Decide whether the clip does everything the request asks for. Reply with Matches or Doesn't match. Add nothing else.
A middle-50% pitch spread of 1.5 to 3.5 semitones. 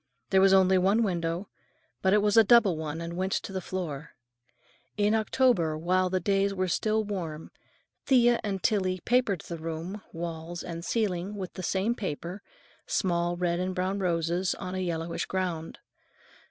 Matches